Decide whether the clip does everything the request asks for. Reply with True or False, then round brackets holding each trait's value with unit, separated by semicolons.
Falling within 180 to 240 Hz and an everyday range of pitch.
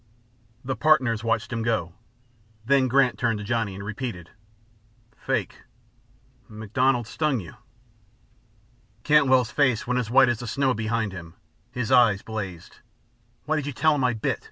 False (120 Hz; 3.4 semitones)